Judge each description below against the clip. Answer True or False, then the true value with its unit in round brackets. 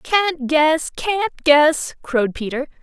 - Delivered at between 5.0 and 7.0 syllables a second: False (3.3 syllables/s)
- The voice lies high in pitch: True (305 Hz)